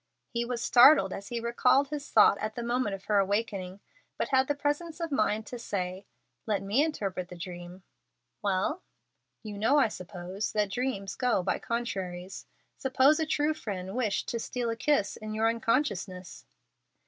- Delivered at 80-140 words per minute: No, average, 170 wpm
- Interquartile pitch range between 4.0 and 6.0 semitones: Yes, average, 4.9 semitones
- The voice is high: Yes, high, 215 Hz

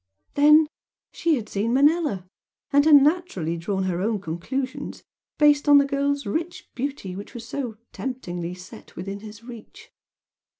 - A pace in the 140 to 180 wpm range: Yes, average, 145 wpm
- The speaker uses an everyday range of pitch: No, wide, 6.6 semitones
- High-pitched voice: Yes, high, 245 Hz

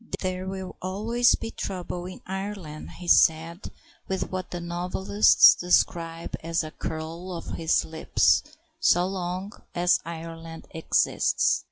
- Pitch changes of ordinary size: No, narrow, 2.2 semitones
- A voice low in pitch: No, medium, 175 Hz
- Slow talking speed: Yes, slow, 130 wpm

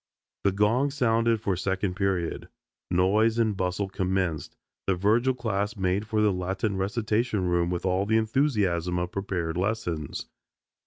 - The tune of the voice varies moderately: Yes, average, 3.3 semitones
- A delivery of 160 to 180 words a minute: No, average, 145 wpm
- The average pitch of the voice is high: No, low, 100 Hz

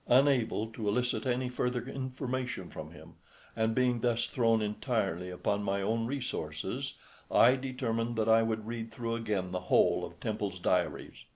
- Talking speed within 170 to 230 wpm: No, average, 160 wpm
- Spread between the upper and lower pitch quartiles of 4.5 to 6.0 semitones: No, narrow, 2.5 semitones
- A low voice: Yes, low, 115 Hz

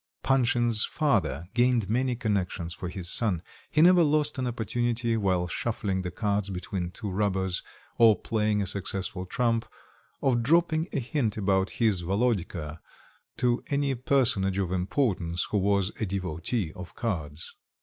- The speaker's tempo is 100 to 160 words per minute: Yes, average, 145 wpm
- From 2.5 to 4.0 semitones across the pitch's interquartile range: No, average, 4.6 semitones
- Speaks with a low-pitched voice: Yes, low, 105 Hz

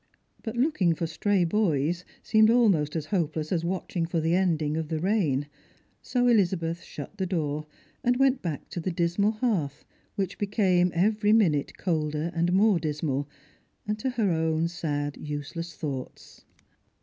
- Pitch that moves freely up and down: No, average, 4.8 semitones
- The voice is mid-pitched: Yes, medium, 170 Hz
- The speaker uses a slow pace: No, average, 155 wpm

